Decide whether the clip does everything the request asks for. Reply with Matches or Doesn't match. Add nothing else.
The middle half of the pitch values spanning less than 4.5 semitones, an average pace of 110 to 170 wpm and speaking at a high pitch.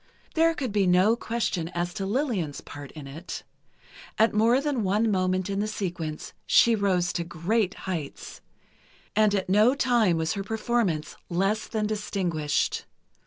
Matches